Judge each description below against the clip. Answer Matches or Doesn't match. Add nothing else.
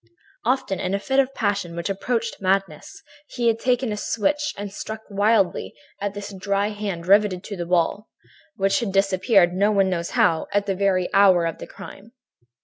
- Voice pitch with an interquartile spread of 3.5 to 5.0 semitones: Doesn't match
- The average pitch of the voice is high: Matches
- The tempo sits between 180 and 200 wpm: Matches